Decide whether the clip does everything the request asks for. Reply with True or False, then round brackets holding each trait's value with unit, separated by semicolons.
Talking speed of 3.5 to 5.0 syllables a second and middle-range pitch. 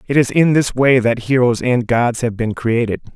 False (4.6 syllables/s; 120 Hz)